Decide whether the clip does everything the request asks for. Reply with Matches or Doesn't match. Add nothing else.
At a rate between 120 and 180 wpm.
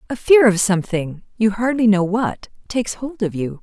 Doesn't match